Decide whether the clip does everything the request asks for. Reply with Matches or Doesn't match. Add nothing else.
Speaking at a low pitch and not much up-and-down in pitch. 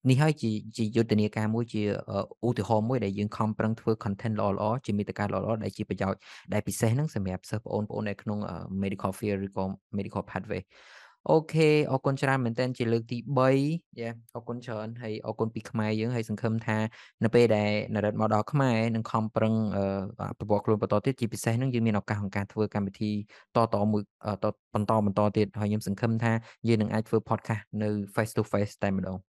Matches